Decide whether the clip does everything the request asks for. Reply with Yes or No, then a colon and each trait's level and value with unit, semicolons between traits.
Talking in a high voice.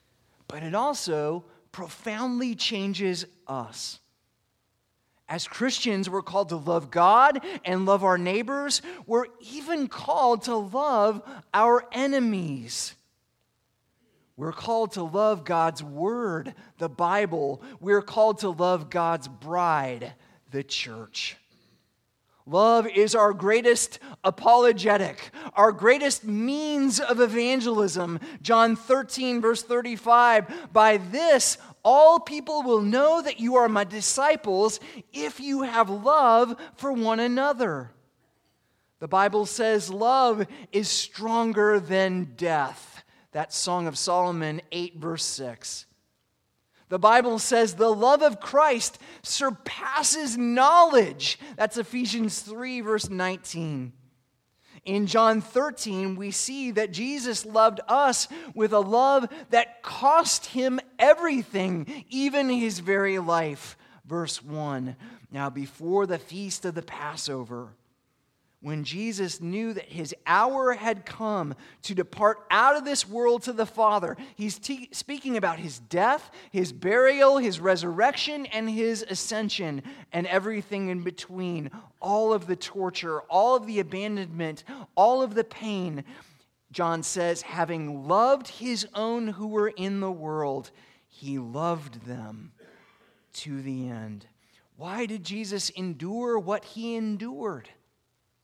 Yes: high, 205 Hz